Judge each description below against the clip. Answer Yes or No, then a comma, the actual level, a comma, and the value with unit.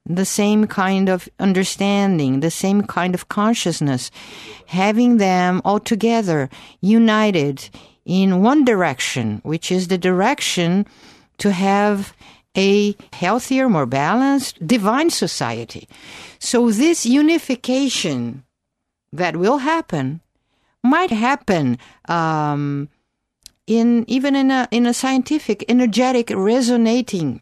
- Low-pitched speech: No, high, 200 Hz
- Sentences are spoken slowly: Yes, slow, 105 wpm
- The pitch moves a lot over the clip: Yes, wide, 6.2 semitones